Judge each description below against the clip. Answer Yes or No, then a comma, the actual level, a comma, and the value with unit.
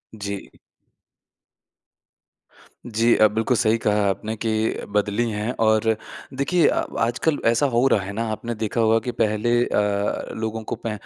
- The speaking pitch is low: Yes, low, 110 Hz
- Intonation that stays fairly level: Yes, narrow, 1.7 semitones